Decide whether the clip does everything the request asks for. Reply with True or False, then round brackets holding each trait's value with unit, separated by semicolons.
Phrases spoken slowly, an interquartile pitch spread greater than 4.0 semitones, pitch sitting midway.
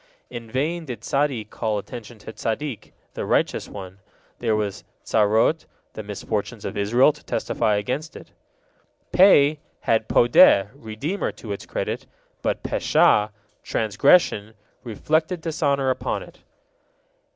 False (125 wpm; 5.5 semitones; 115 Hz)